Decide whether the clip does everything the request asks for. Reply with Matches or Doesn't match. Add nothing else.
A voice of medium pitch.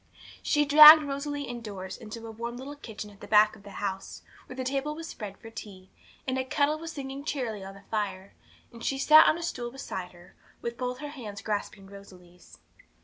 Doesn't match